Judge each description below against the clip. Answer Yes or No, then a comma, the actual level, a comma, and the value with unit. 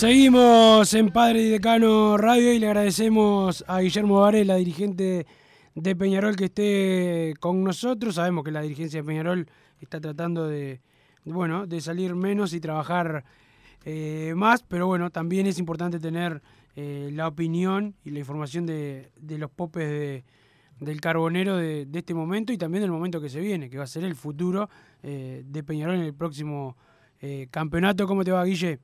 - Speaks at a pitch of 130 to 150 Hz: No, medium, 170 Hz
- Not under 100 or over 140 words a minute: No, average, 175 wpm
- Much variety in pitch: No, average, 4.4 semitones